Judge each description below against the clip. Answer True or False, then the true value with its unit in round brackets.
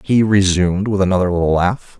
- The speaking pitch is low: True (95 Hz)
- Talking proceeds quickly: False (180 wpm)